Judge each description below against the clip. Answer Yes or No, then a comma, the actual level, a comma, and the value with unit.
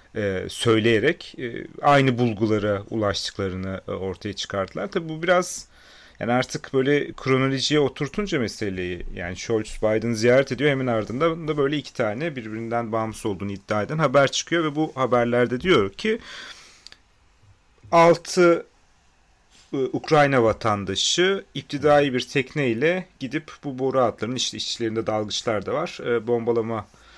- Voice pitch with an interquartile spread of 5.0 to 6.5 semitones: Yes, average, 5.3 semitones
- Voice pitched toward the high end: No, low, 125 Hz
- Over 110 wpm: Yes, average, 130 wpm